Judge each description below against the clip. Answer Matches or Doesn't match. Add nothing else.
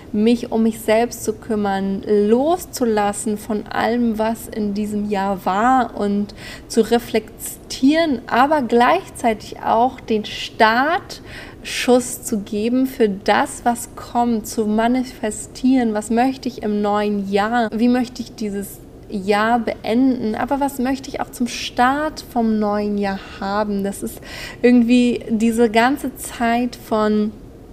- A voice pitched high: Matches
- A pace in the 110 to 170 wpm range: Matches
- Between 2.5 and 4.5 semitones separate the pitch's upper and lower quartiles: Matches